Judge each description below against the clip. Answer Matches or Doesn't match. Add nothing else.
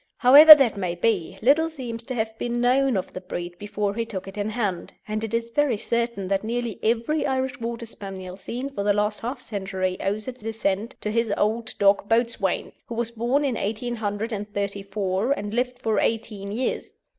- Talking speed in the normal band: Matches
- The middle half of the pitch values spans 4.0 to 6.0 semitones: Doesn't match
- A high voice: Matches